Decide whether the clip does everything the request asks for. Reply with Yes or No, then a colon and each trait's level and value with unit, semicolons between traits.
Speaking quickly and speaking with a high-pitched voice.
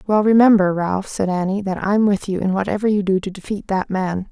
Yes: fast, 235 wpm; high, 195 Hz